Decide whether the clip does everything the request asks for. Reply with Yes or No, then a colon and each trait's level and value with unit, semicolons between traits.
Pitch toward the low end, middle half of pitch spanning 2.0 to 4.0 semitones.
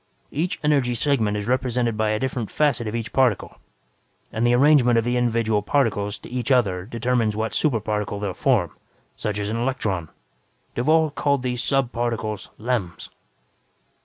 Yes: low, 120 Hz; average, 3.4 semitones